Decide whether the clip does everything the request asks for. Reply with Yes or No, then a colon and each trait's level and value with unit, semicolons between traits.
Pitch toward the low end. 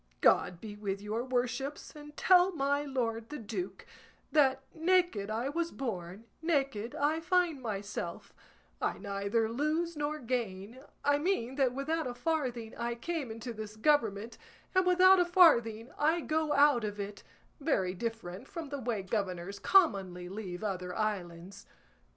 No: high, 240 Hz